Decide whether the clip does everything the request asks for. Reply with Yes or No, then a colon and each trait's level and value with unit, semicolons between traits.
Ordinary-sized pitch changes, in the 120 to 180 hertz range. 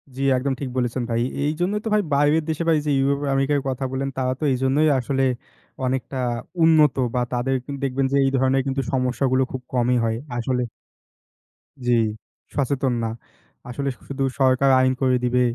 No: narrow, 1.7 semitones; low, 135 Hz